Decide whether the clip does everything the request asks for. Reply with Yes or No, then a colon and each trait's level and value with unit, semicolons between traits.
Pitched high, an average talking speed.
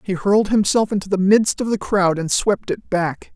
No: high, 195 Hz; fast, 235 wpm